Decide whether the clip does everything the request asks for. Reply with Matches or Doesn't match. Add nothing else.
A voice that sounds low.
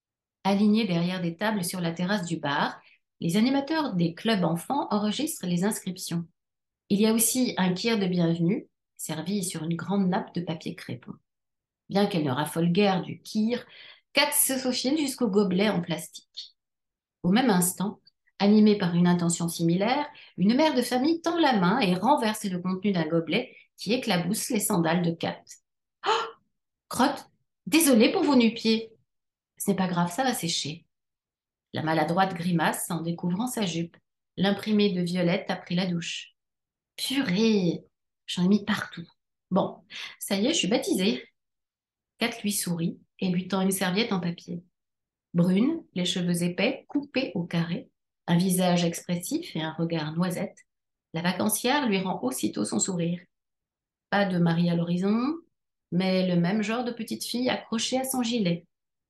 Doesn't match